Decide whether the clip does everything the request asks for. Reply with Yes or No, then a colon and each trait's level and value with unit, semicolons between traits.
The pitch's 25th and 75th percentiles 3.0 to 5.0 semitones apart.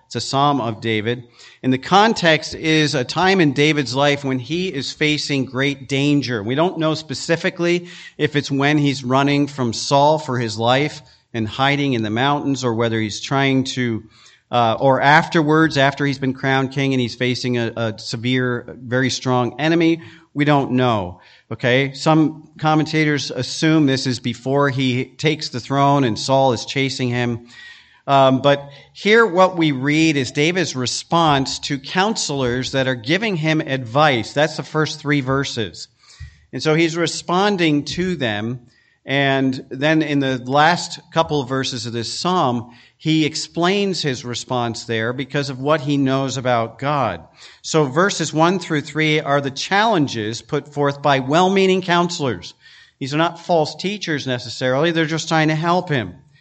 Yes: average, 3.7 semitones